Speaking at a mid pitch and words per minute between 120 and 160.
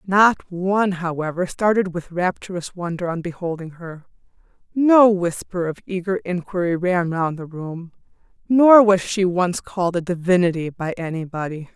Yes: medium, 180 Hz; average, 145 wpm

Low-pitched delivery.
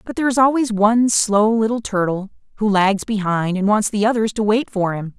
No: high, 210 Hz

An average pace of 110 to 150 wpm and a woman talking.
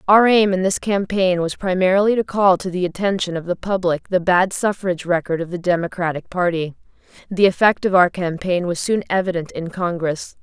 No: average, 190 wpm; female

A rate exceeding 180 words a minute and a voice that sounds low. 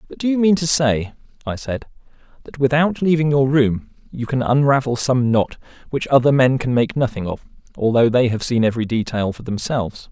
Yes: average, 195 wpm; low, 130 Hz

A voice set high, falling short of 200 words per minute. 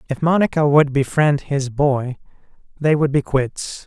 No: medium, 140 Hz; average, 155 wpm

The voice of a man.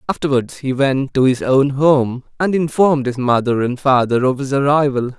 Yes: male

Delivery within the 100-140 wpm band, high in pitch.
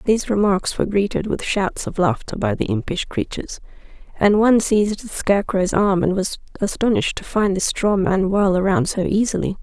No: average, 185 wpm; high, 200 Hz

